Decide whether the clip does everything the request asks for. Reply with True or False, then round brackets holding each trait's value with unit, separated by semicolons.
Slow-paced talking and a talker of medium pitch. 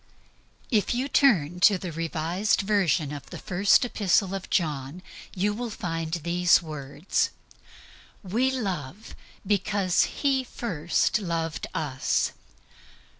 True (110 wpm; 180 Hz)